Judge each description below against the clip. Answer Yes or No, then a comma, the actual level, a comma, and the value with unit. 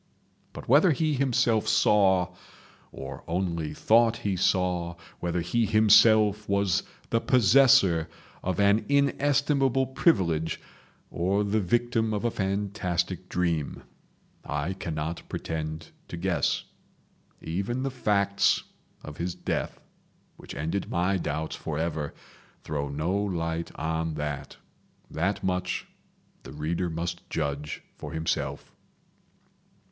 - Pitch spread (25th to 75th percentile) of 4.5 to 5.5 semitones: Yes, average, 4.9 semitones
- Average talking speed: No, slow, 110 wpm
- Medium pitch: No, very low, 95 Hz